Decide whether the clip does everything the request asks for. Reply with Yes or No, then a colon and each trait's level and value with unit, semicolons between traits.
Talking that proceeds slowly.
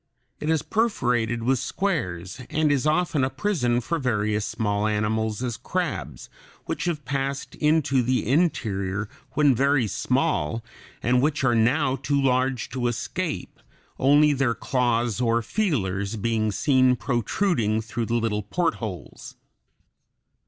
Yes: slow, 130 wpm